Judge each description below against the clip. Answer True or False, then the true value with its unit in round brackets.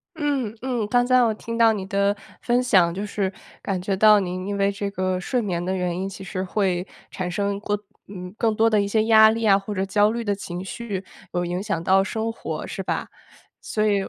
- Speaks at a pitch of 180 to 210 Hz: True (200 Hz)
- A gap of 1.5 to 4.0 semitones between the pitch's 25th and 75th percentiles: True (2.8 semitones)